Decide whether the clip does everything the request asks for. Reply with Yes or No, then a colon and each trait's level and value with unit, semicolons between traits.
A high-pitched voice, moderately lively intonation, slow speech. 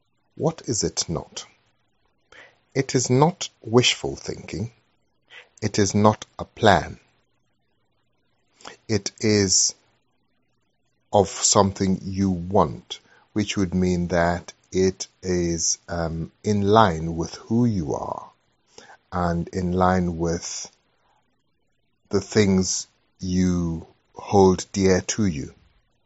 No: very low, 95 Hz; average, 3.2 semitones; slow, 100 wpm